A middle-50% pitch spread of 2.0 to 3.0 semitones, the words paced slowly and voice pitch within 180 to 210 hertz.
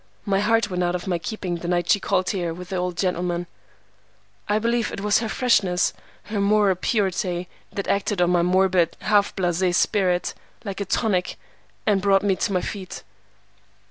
No: narrow, 2.5 semitones; average, 180 wpm; high, 190 Hz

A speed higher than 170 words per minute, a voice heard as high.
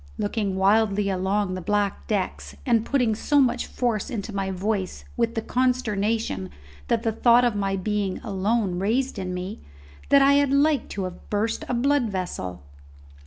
No: average, 165 wpm; high, 210 Hz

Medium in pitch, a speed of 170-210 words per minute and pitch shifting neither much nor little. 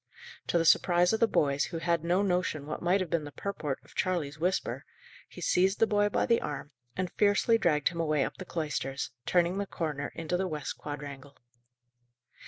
Yes: medium, 170 Hz; average, 195 wpm; average, 3.9 semitones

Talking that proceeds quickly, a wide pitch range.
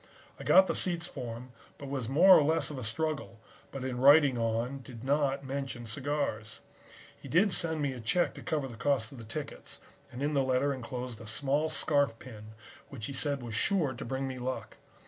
No: fast, 210 wpm; average, 3.2 semitones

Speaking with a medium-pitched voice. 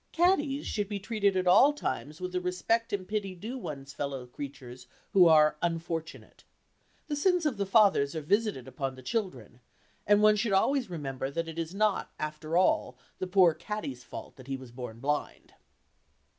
Yes: medium, 180 Hz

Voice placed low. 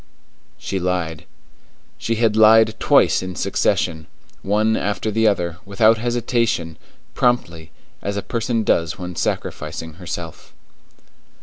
Yes: low, 100 Hz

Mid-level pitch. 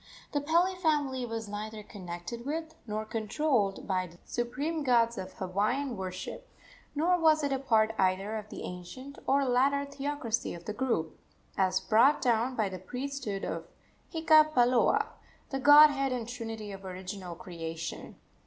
No: high, 235 Hz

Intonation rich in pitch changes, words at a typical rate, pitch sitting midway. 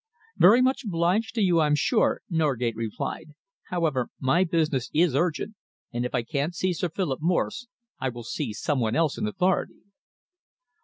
Yes: wide, 5.7 semitones; average, 165 wpm; medium, 160 Hz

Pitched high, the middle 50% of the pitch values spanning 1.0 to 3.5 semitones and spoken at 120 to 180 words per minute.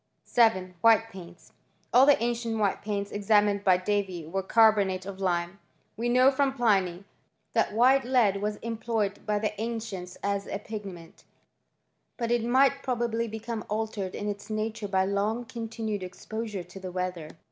Yes: high, 210 Hz; average, 3.0 semitones; average, 160 wpm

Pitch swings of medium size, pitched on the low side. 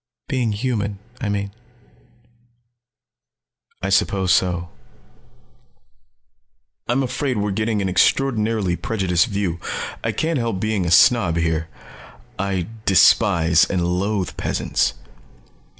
Yes: average, 3.9 semitones; low, 100 Hz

